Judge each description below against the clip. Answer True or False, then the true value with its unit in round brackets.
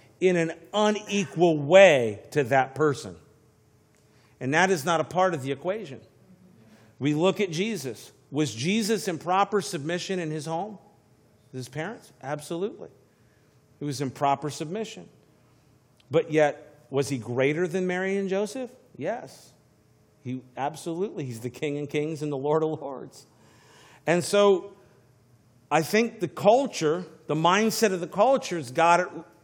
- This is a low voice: False (155 Hz)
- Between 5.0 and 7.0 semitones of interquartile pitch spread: True (5.3 semitones)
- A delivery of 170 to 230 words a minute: False (145 wpm)